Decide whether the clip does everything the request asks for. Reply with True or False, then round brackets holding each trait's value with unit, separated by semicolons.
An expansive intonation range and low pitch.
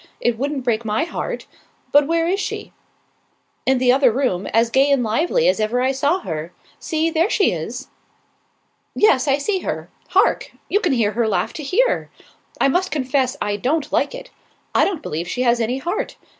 False (6.0 semitones; 265 Hz)